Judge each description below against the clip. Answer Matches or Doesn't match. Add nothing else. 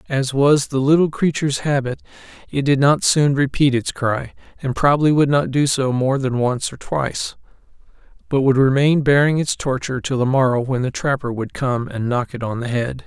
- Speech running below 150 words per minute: Doesn't match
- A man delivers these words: Matches